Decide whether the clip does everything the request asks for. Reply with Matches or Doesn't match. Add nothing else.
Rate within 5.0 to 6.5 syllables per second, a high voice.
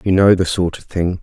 Doesn't match